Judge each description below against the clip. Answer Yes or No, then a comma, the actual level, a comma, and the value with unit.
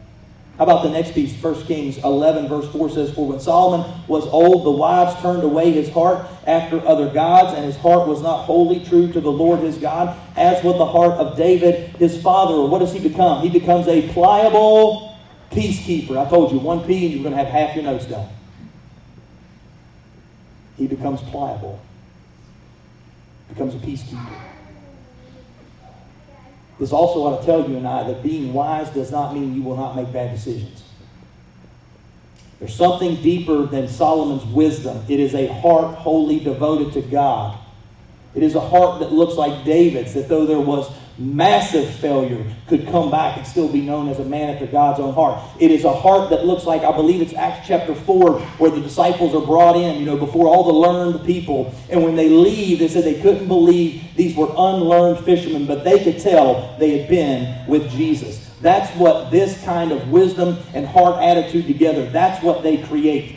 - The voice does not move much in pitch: No, average, 3.8 semitones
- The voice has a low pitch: No, medium, 155 Hz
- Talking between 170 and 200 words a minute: Yes, average, 185 wpm